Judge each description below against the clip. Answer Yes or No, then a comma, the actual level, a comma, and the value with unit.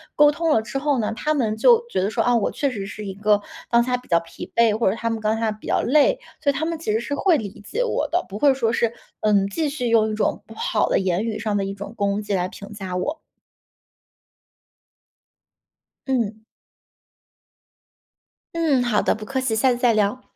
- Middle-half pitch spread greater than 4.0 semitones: Yes, average, 5.0 semitones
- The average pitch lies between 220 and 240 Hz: Yes, high, 225 Hz